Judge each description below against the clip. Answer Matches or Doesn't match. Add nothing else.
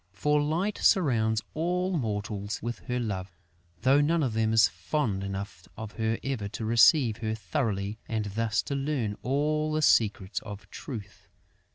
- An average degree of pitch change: Doesn't match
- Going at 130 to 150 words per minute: Doesn't match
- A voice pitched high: Doesn't match